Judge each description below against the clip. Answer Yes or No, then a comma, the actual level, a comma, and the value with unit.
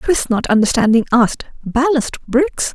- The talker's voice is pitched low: No, very high, 255 Hz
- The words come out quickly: No, slow, 130 wpm